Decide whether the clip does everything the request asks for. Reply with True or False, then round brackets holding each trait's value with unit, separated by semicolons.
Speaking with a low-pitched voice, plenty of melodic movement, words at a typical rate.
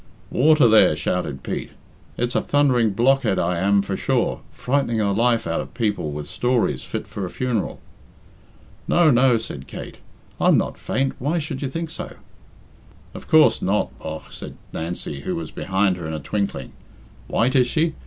True (110 Hz; 6.6 semitones; 175 wpm)